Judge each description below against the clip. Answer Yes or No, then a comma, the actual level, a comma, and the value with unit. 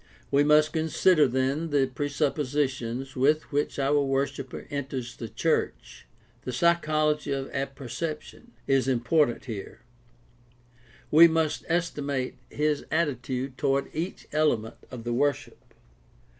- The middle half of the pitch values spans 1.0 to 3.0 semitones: Yes, average, 2.7 semitones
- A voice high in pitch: No, medium, 140 Hz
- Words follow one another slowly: Yes, slow, 115 wpm